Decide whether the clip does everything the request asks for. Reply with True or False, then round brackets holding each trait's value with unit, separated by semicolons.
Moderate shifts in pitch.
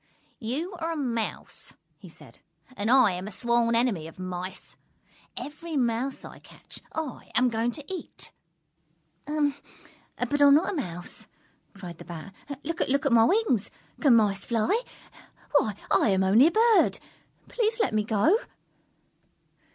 False (6.4 semitones)